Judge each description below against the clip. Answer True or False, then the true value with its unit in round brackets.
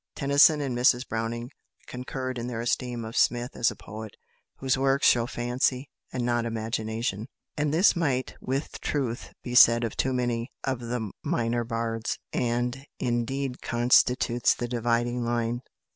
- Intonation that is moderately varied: False (1.7 semitones)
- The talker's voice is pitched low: True (120 Hz)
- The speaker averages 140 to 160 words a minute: True (150 wpm)